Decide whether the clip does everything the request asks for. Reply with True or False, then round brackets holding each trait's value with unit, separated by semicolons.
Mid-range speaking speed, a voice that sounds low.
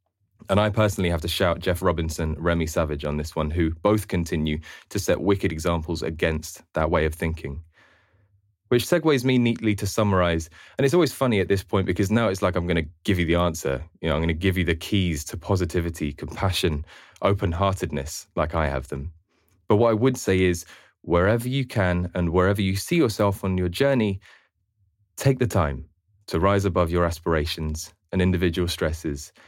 True (195 wpm; 90 Hz)